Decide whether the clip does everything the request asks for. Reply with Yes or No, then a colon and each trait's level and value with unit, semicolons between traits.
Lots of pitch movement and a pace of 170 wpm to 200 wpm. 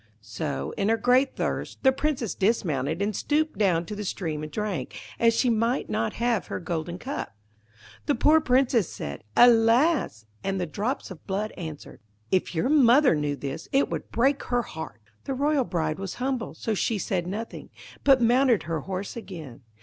Yes: wide, 6.8 semitones; average, 180 wpm